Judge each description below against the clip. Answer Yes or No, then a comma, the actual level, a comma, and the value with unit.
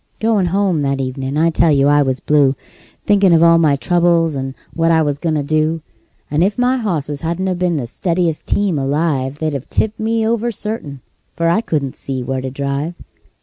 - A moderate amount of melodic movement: Yes, average, 4.5 semitones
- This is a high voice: No, medium, 160 Hz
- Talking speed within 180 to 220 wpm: Yes, average, 200 wpm